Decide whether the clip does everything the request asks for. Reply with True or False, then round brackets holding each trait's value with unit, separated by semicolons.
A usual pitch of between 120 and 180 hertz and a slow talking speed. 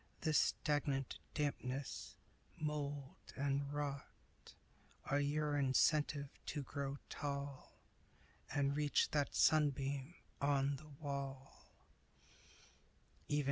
True (140 Hz; 85 wpm)